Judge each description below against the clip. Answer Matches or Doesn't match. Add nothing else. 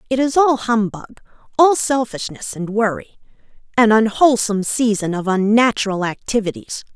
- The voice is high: Matches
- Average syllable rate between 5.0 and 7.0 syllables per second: Matches